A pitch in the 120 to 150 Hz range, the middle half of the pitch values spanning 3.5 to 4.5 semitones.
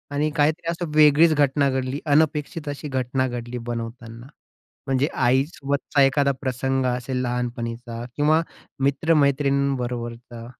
No: low, 135 Hz; average, 3.0 semitones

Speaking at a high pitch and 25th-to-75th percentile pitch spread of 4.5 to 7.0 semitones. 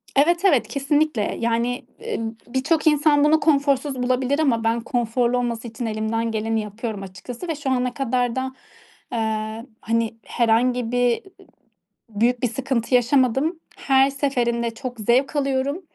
No: high, 245 Hz; average, 3.3 semitones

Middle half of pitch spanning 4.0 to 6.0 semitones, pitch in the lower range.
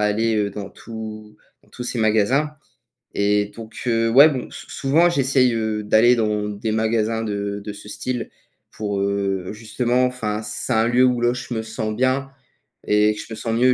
No: average, 2.8 semitones; low, 110 Hz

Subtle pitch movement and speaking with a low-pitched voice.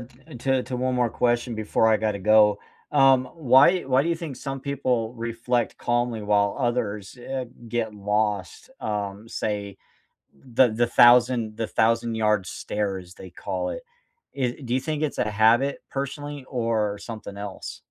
No: average, 3.4 semitones; low, 115 Hz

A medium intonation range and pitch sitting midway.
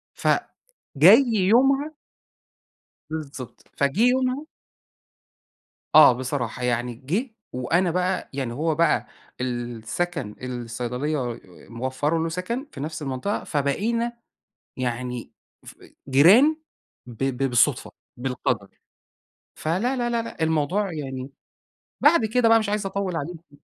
No: wide, 8.3 semitones; medium, 155 Hz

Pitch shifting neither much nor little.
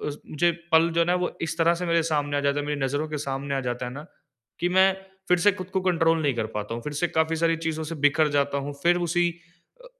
Yes: average, 3.1 semitones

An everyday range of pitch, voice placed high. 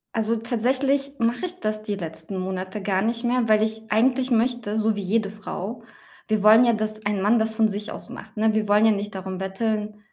No: narrow, 2.0 semitones; high, 215 Hz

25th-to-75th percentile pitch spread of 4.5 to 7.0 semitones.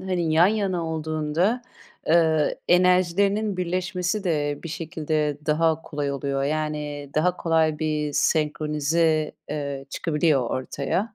No: average, 2.9 semitones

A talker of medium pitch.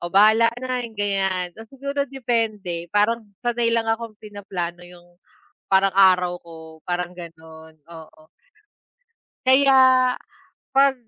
No: high, 200 Hz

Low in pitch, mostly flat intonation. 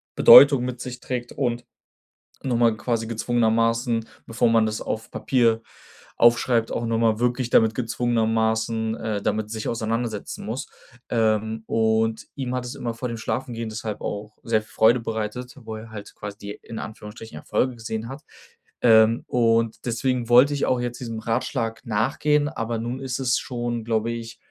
Yes: low, 115 Hz; narrow, 1.6 semitones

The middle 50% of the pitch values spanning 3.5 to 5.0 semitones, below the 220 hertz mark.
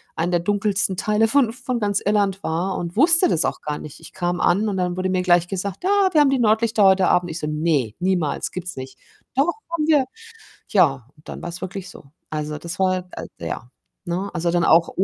Yes: average, 3.8 semitones; medium, 185 Hz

